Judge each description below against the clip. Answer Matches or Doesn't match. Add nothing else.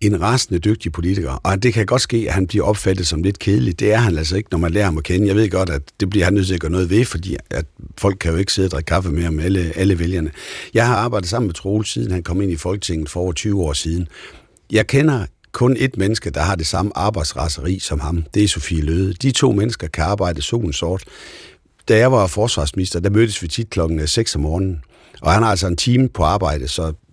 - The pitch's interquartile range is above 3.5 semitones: Matches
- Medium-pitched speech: Doesn't match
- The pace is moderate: Doesn't match